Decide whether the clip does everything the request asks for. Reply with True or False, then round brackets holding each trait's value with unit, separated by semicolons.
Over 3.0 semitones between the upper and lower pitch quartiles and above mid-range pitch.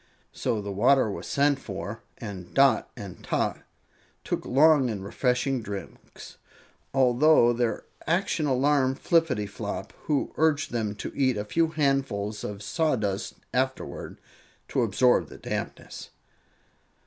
False (5.2 semitones; 125 Hz)